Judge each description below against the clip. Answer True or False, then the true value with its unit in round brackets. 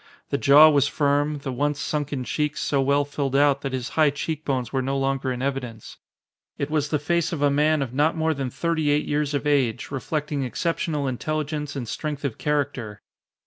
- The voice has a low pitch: False (145 Hz)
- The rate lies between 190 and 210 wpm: True (200 wpm)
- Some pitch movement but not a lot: False (1.8 semitones)